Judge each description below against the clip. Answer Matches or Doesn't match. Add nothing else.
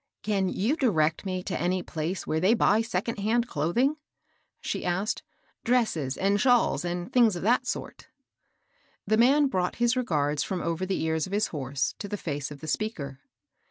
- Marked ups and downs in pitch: Matches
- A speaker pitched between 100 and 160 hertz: Doesn't match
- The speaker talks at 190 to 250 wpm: Matches